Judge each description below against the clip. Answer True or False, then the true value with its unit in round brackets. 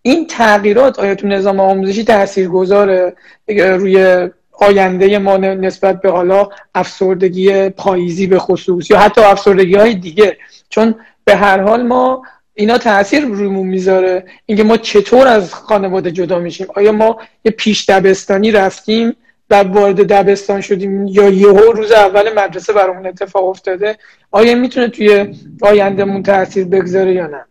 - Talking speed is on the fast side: False (140 wpm)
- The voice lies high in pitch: True (200 Hz)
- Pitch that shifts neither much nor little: False (1.9 semitones)